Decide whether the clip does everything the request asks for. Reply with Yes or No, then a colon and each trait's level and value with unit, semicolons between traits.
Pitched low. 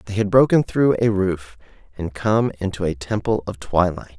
Yes: low, 100 Hz